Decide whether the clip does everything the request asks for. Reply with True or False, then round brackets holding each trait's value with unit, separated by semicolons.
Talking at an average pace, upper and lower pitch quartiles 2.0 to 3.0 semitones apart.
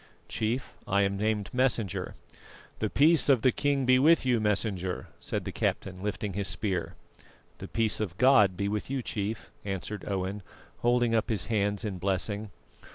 False (165 wpm; 3.6 semitones)